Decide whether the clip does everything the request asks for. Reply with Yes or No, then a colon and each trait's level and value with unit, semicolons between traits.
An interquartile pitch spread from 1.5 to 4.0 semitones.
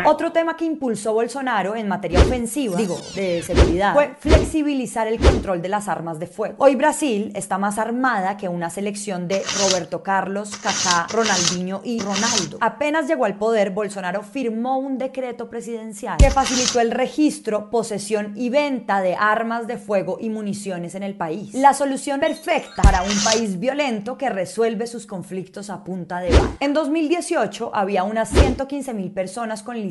No: average, 4.9 semitones